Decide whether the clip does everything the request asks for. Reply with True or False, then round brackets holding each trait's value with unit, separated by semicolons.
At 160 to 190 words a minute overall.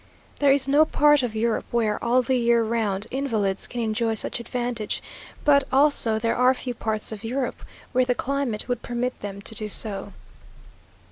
True (180 wpm)